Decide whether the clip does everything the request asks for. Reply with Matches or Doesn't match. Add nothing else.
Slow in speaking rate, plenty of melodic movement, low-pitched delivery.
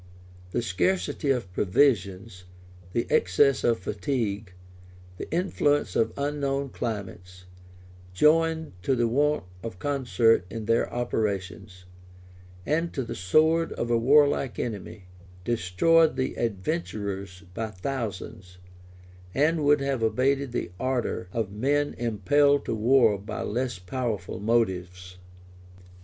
Matches